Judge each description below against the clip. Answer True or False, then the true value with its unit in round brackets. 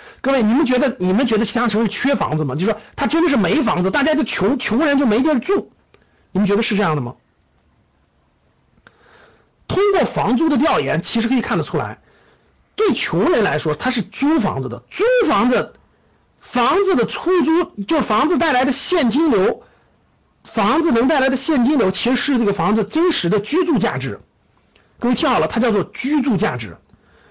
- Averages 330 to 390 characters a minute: False (280 characters per minute)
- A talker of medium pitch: False (255 Hz)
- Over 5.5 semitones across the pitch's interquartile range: True (6.6 semitones)